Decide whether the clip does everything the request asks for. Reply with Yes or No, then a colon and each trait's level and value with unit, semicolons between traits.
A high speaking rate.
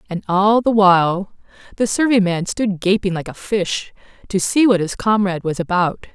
No: average, 185 wpm